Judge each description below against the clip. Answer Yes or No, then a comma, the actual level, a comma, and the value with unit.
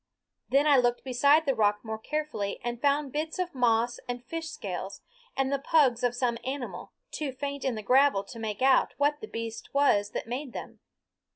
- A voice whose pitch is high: Yes, very high, 255 Hz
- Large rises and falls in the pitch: No, average, 3.8 semitones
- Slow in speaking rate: No, average, 195 wpm